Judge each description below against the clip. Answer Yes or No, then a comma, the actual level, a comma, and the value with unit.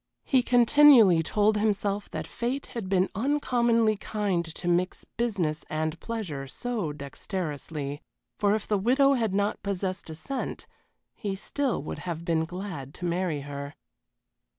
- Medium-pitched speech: No, high, 195 Hz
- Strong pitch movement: Yes, wide, 6.0 semitones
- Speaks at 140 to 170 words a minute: Yes, average, 145 wpm